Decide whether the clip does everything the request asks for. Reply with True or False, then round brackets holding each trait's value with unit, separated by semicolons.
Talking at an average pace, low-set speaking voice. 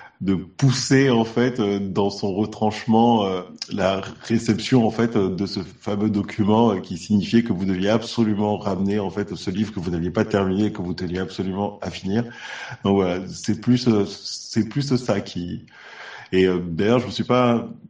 True (200 wpm; 105 Hz)